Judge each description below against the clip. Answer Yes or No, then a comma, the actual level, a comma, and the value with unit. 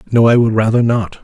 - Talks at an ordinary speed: No, fast, 245 wpm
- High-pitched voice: No, low, 115 Hz